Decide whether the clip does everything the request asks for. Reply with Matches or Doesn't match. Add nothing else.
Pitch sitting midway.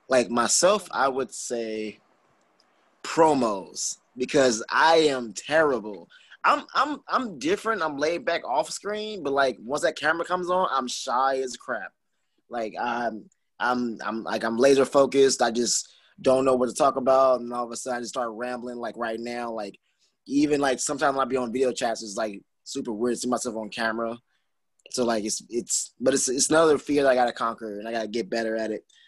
Doesn't match